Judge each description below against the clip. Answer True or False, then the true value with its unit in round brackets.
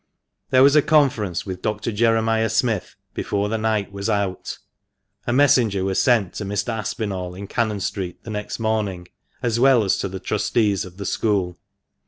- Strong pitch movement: False (2.6 semitones)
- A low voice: True (105 Hz)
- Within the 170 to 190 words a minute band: True (175 wpm)